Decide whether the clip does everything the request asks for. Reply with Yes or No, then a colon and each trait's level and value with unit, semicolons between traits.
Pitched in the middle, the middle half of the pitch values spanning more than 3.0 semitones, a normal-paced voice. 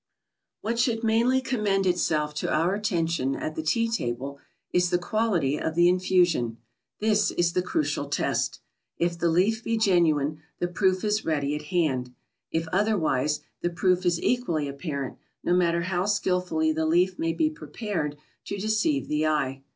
Yes: medium, 175 Hz; average, 5.0 semitones; average, 165 wpm